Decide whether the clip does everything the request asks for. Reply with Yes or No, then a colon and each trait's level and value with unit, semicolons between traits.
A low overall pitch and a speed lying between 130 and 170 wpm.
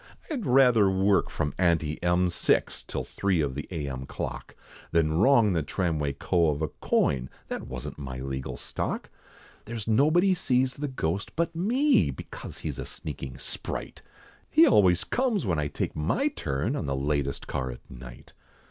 Yes: very low, 85 Hz; average, 165 wpm